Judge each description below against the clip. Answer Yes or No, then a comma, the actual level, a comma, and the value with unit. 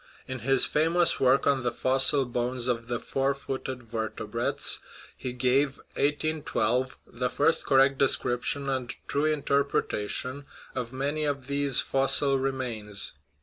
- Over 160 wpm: No, slow, 135 wpm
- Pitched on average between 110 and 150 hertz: Yes, low, 135 Hz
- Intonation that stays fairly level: Yes, narrow, 2.2 semitones